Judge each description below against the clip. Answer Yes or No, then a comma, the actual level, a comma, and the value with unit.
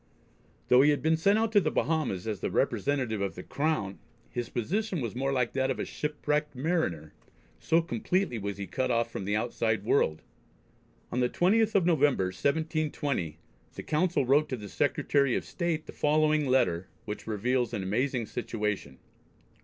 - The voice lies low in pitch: Yes, low, 130 Hz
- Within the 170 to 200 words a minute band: Yes, average, 175 wpm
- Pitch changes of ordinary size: No, wide, 6.3 semitones